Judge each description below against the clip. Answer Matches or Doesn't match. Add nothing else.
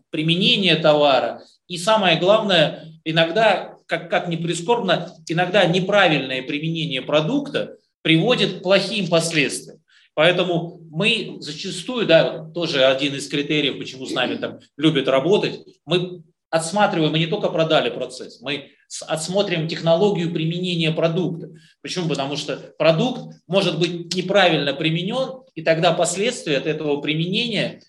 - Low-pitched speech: Doesn't match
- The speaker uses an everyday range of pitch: Matches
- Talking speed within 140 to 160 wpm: Doesn't match